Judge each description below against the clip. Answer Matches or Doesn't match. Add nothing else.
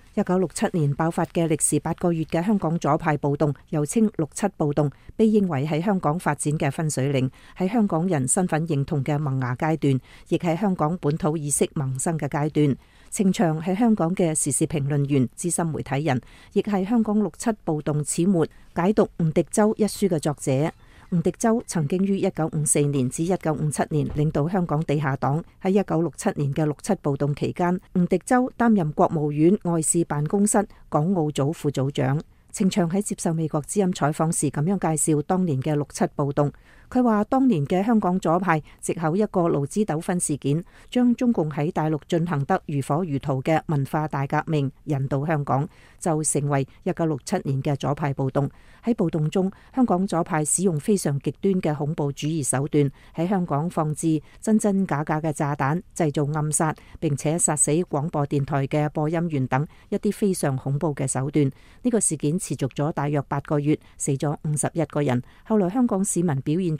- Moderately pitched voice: Matches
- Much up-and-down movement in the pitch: Doesn't match